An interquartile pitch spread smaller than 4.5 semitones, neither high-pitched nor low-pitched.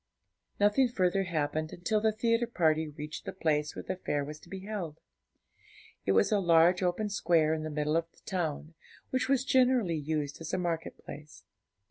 No: average, 4.9 semitones; medium, 170 Hz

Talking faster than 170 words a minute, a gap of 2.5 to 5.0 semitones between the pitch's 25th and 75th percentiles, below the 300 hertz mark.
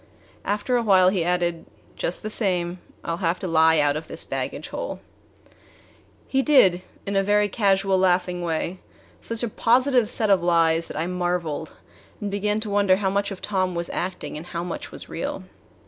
Yes: average, 190 wpm; average, 3.1 semitones; medium, 185 Hz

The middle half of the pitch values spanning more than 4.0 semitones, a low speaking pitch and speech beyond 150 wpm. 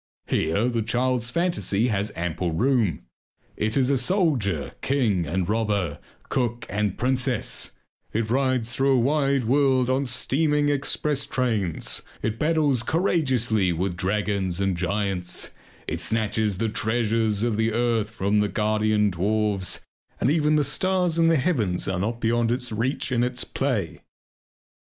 No: average, 4.4 semitones; low, 115 Hz; average, 145 wpm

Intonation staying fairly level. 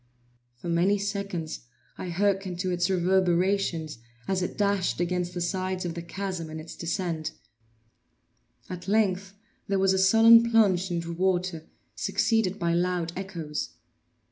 Yes: narrow, 2.3 semitones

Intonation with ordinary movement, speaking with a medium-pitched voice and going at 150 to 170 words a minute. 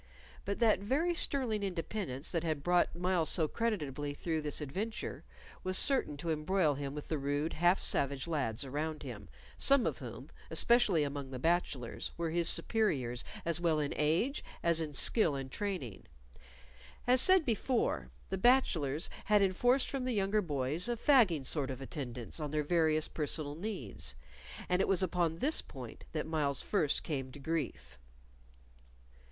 No: wide, 5.8 semitones; medium, 160 Hz; average, 160 wpm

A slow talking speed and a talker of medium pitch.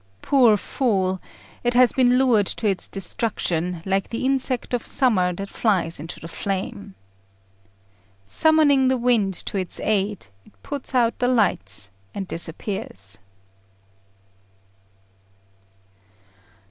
No: slow, 115 wpm; high, 205 Hz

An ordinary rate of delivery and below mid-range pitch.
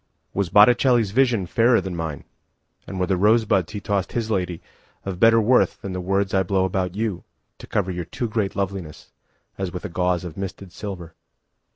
Yes: average, 155 wpm; very low, 95 Hz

